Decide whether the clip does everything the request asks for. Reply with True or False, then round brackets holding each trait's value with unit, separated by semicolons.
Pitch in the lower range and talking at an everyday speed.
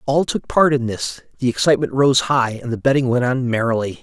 False (125 Hz; 225 wpm)